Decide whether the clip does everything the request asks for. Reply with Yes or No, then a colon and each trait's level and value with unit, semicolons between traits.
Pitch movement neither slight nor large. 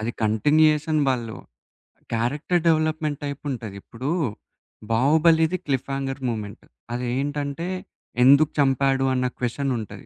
Yes: average, 3.8 semitones